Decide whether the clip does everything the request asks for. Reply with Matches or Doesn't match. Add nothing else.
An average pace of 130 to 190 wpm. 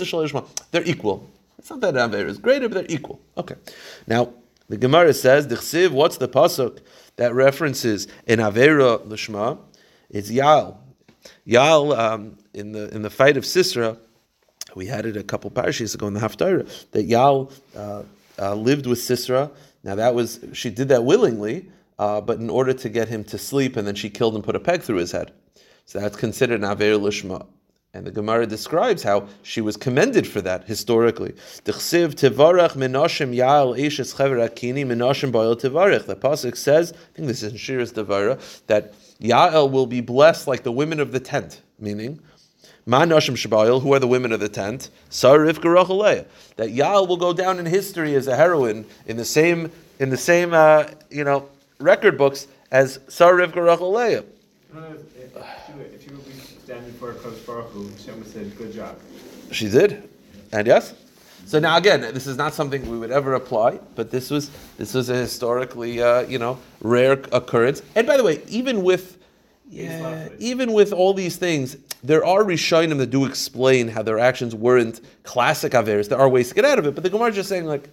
Matches